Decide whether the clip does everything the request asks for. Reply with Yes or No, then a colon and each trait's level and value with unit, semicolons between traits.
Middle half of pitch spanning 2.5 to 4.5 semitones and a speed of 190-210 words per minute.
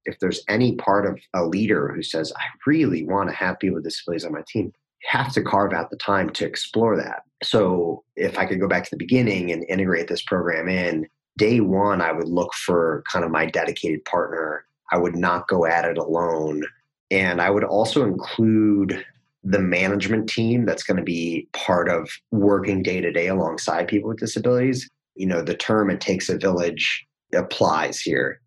Yes: average, 3.7 semitones; average, 195 wpm